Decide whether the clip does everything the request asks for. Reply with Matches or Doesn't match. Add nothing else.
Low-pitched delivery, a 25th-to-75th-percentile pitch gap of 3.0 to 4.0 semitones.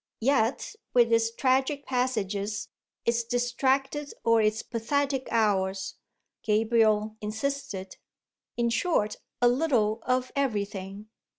Doesn't match